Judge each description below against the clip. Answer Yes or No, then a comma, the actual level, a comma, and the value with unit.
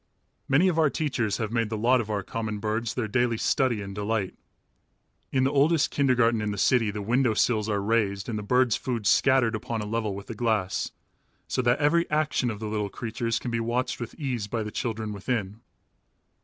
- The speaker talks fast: Yes, fast, 210 wpm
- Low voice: Yes, low, 115 Hz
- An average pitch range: Yes, average, 3.1 semitones